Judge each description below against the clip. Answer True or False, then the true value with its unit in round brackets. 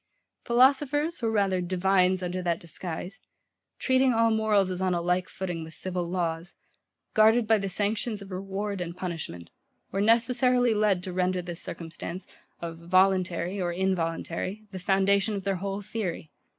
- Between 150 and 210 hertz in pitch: True (190 Hz)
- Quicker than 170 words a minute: False (155 wpm)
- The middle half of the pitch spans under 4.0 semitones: True (3.3 semitones)